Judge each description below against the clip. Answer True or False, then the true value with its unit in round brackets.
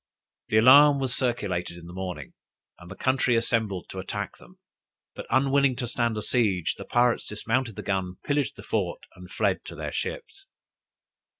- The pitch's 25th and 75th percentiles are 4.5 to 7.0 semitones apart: True (5.5 semitones)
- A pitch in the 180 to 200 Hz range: False (115 Hz)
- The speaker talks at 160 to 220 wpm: True (175 wpm)